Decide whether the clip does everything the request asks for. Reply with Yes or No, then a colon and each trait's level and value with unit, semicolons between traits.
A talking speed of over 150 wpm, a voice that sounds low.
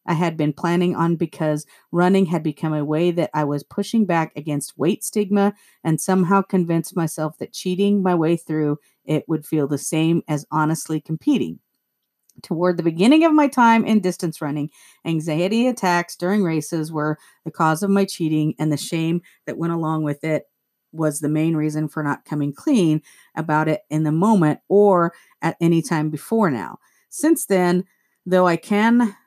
No: average, 180 wpm; medium, 165 Hz